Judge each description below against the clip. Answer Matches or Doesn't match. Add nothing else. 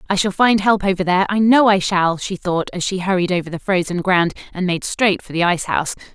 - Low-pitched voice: Doesn't match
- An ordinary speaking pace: Doesn't match